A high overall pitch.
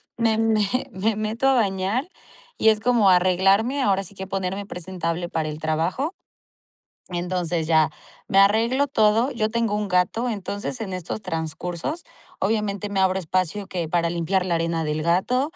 Yes: high, 195 Hz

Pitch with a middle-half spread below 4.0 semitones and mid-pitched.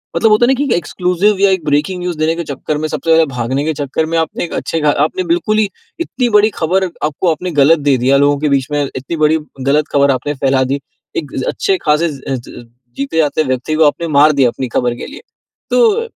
No: average, 4.3 semitones; medium, 155 Hz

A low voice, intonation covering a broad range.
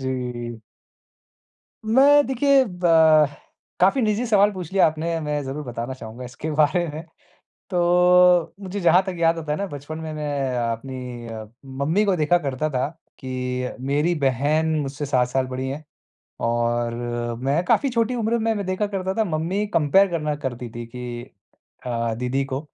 No: medium, 150 Hz; wide, 6.0 semitones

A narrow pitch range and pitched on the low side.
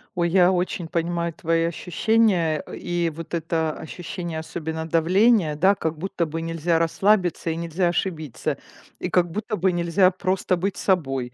No: narrow, 2.2 semitones; medium, 170 Hz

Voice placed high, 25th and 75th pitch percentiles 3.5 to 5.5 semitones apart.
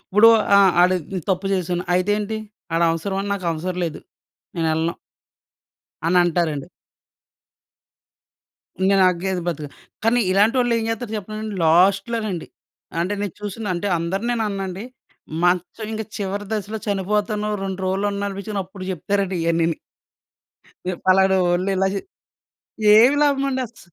No: high, 195 Hz; average, 2.9 semitones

